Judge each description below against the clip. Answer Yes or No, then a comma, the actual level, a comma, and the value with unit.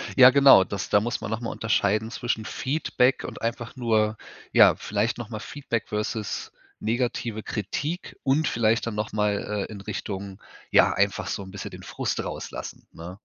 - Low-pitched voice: Yes, low, 110 Hz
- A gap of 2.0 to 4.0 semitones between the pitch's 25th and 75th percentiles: Yes, narrow, 2.4 semitones